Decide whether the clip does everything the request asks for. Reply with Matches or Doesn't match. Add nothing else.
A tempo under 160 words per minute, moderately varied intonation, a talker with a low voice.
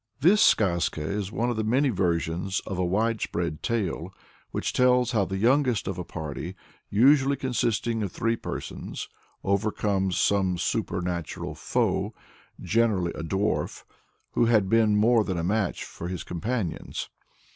Matches